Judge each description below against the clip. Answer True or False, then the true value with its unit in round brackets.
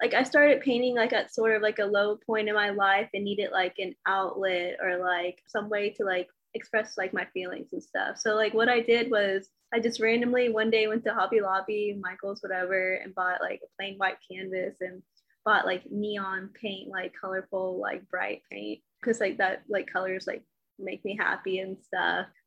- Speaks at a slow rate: False (205 wpm)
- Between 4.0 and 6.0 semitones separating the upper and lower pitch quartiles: False (2.8 semitones)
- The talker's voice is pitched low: False (200 Hz)